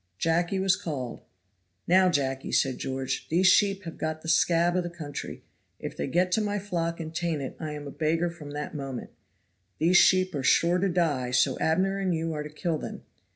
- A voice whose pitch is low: No, medium, 165 Hz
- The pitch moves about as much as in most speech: Yes, average, 3.5 semitones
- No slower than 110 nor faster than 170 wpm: No, fast, 205 wpm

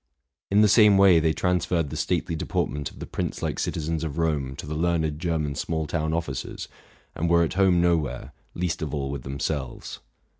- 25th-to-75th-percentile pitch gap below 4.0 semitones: Yes, average, 2.7 semitones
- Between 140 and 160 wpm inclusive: No, average, 190 wpm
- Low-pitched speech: Yes, very low, 80 Hz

